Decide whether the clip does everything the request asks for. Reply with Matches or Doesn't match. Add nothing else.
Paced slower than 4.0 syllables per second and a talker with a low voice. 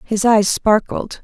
Doesn't match